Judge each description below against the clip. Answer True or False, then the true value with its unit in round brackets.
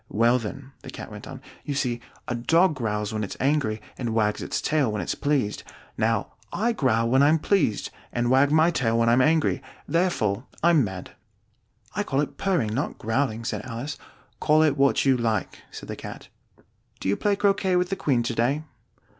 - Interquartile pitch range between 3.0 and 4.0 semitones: False (5.2 semitones)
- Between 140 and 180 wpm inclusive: False (195 wpm)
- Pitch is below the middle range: True (130 Hz)